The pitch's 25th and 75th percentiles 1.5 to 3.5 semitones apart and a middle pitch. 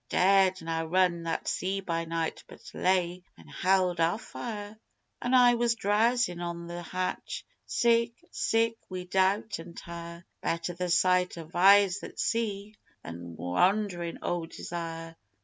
Yes: average, 3.2 semitones; medium, 180 Hz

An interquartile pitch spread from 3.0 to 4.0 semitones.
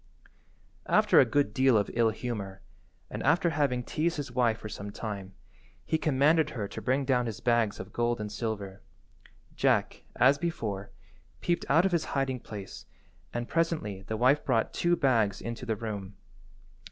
No: average, 5.1 semitones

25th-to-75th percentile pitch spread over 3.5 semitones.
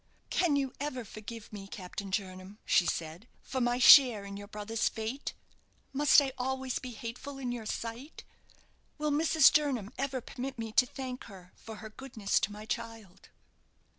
Yes: average, 4.3 semitones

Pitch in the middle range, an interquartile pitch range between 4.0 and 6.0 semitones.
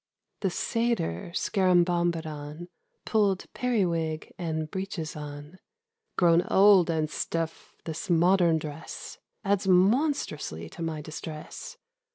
No: medium, 170 Hz; average, 3.6 semitones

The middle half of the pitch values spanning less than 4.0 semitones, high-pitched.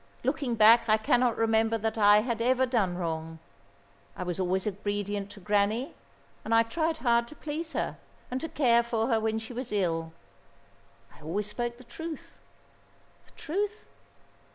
Yes: average, 3.3 semitones; high, 225 Hz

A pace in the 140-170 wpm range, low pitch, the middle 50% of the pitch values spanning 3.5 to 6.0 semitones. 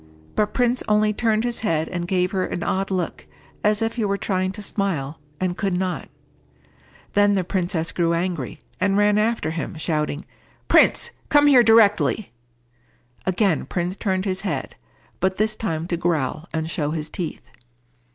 No: average, 165 wpm; high, 190 Hz; average, 3.8 semitones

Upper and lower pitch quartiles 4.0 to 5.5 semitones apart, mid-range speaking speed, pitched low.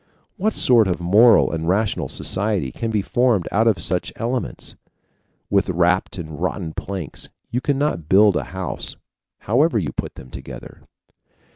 Yes: average, 4.6 semitones; average, 150 wpm; low, 100 Hz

